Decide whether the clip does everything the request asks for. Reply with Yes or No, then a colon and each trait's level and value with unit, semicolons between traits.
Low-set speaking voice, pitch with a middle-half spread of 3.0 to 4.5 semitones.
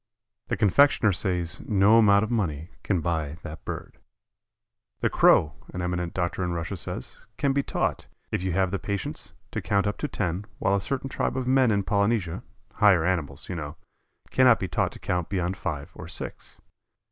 Yes: very low, 95 Hz; average, 3.5 semitones